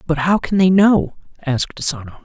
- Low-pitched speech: No, medium, 165 Hz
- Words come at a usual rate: Yes, average, 190 wpm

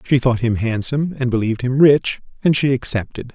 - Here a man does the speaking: Yes, male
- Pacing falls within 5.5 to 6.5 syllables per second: Yes, 5.7 syllables/s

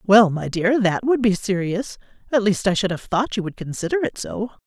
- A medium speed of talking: No, fast, 230 wpm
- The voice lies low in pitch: No, high, 205 Hz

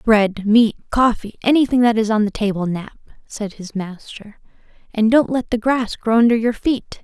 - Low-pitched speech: No, high, 225 Hz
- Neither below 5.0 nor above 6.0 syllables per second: No, 4.6 syllables/s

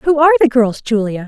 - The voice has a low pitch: No, very high, 255 Hz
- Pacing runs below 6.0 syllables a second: No, 6.3 syllables/s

